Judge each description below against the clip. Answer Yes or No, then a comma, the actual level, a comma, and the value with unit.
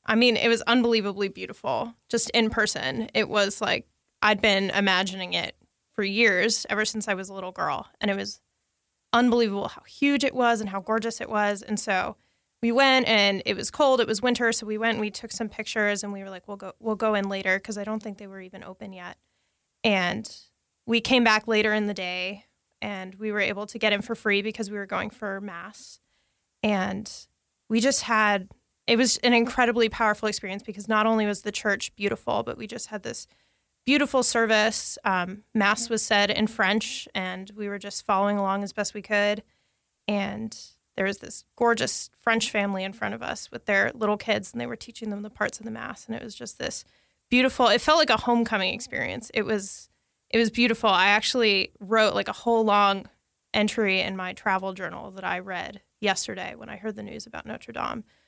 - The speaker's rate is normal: No, fast, 210 wpm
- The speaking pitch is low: No, high, 215 Hz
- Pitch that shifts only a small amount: Yes, narrow, 2.3 semitones